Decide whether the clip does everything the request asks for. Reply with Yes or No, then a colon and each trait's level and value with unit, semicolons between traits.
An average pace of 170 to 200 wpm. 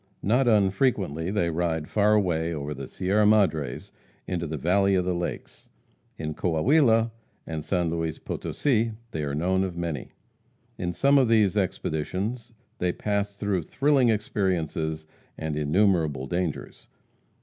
No: average, 140 wpm